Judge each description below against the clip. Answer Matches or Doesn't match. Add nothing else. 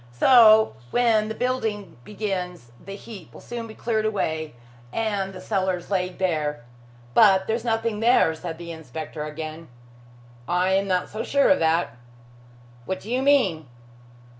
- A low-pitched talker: Doesn't match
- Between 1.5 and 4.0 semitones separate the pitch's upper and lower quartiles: Doesn't match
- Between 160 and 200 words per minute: Doesn't match